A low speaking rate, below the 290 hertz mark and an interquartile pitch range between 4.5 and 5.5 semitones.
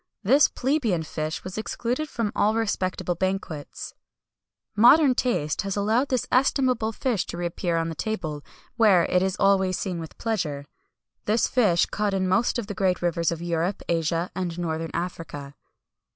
No: average, 165 wpm; high, 190 Hz; average, 4.8 semitones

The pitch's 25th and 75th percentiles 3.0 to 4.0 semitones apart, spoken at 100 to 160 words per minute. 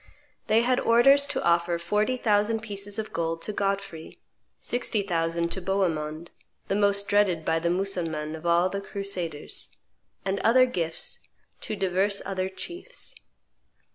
Yes: average, 3.6 semitones; average, 140 wpm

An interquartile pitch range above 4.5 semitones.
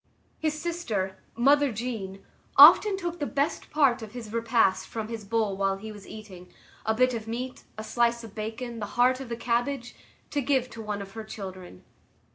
No: average, 3.3 semitones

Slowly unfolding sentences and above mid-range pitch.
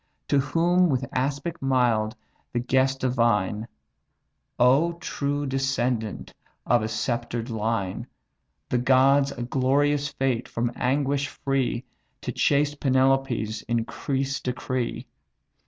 No: slow, 105 wpm; low, 130 Hz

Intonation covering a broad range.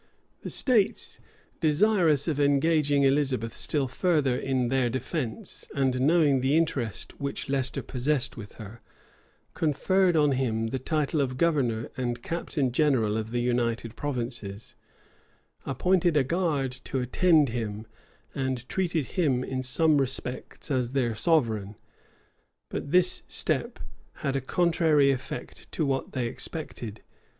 No: average, 4.1 semitones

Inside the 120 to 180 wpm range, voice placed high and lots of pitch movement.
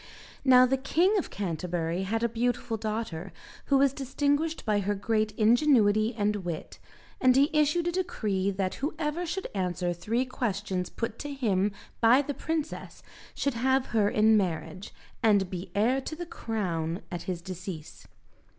Yes: average, 160 wpm; high, 220 Hz; wide, 6.1 semitones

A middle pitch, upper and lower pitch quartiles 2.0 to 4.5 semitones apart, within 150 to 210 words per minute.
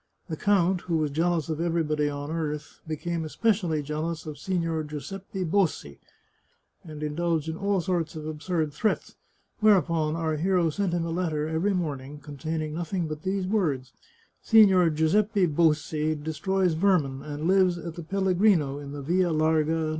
Yes: medium, 165 Hz; average, 3.1 semitones; average, 165 wpm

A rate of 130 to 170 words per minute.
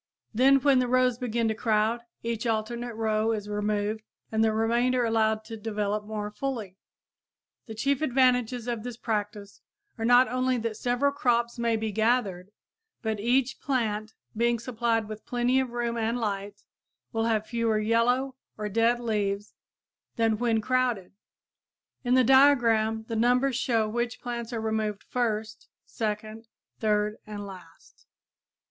Yes: average, 150 wpm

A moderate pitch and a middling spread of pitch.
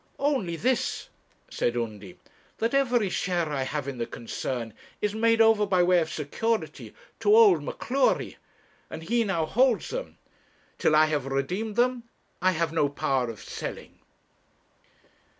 No: medium, 180 Hz; wide, 8.2 semitones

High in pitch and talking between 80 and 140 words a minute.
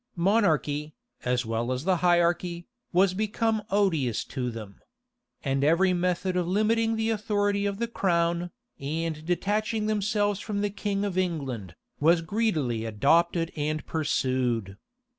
No: medium, 175 Hz; slow, 135 wpm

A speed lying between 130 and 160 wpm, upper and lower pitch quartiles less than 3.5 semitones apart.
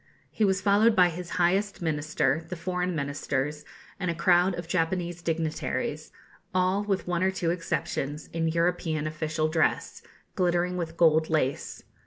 Yes: average, 150 wpm; narrow, 2.4 semitones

